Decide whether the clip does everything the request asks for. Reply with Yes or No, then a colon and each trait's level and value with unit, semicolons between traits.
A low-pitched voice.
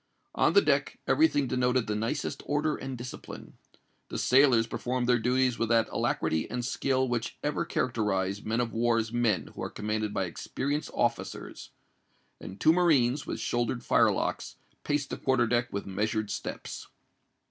Yes: low, 120 Hz